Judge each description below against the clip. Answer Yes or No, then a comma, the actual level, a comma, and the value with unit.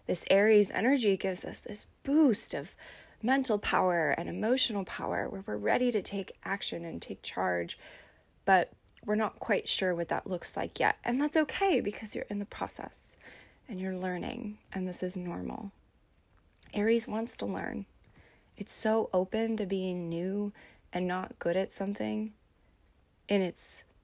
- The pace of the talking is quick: No, average, 160 wpm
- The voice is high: Yes, high, 205 Hz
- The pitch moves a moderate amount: Yes, average, 3.6 semitones